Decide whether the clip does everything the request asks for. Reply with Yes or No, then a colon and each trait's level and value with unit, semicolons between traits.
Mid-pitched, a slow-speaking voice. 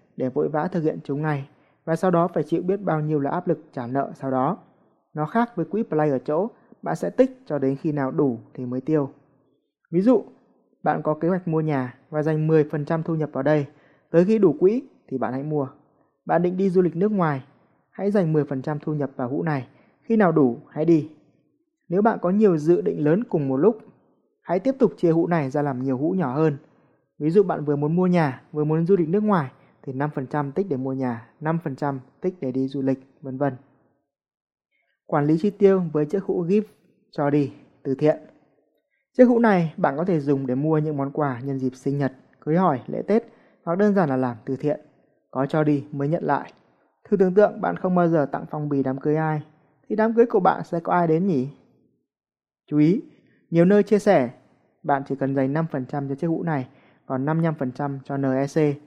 No: medium, 155 Hz; average, 225 wpm